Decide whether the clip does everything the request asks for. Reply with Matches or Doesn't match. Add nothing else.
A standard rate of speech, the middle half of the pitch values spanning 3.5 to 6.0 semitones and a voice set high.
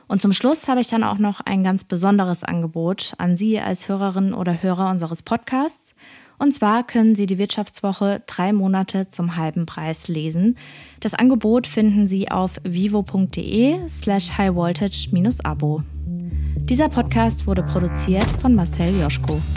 Matches